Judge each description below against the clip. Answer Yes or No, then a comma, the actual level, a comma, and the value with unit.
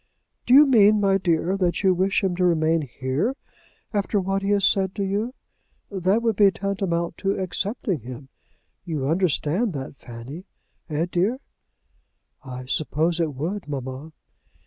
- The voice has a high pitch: No, medium, 180 Hz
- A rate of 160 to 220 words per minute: No, average, 150 wpm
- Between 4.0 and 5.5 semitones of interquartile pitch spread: Yes, average, 4.3 semitones